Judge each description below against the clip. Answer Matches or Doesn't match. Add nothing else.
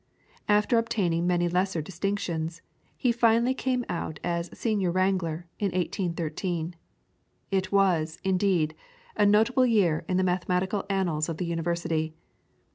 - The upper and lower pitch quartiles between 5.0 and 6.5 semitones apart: Doesn't match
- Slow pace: Matches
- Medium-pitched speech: Matches